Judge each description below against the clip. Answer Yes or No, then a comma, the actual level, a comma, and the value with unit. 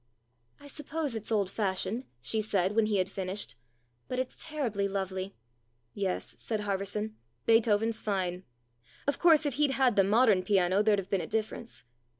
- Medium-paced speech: Yes, average, 170 wpm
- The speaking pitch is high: Yes, high, 210 Hz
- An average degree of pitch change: Yes, average, 3.4 semitones